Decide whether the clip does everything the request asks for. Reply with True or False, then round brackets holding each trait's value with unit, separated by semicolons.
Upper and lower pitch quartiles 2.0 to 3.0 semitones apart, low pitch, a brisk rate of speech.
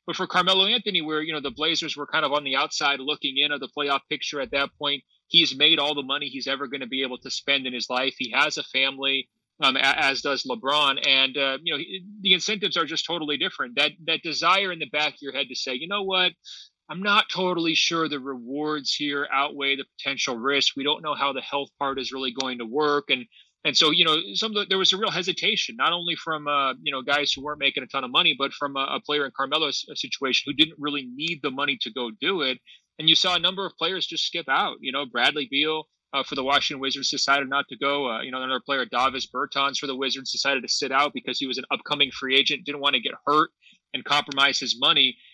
False (2.6 semitones; 145 Hz; 255 wpm)